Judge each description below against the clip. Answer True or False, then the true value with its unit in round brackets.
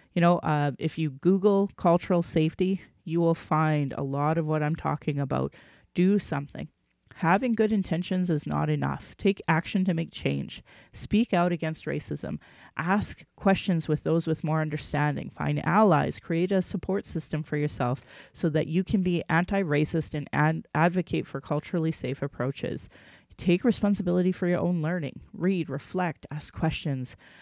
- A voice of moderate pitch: True (165 Hz)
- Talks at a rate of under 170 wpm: True (160 wpm)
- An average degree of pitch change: True (3.4 semitones)